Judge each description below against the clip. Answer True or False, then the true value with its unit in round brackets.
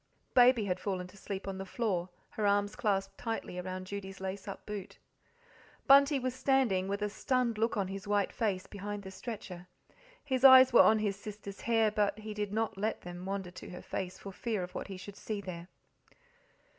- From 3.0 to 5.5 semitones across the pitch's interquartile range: False (2.6 semitones)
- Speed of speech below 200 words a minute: False (205 wpm)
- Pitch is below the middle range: False (200 Hz)